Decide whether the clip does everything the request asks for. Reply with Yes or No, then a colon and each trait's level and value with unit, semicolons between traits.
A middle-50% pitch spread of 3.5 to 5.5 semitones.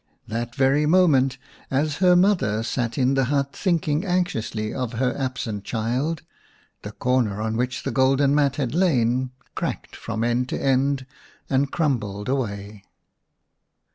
Yes: average, 3.8 semitones